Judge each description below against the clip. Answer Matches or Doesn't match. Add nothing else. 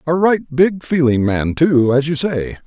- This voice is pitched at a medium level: Matches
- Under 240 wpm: Matches